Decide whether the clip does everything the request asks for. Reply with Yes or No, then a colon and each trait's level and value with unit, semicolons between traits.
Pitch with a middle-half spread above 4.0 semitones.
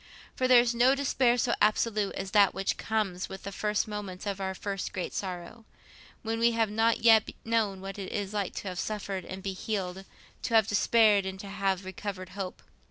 No: narrow, 2.6 semitones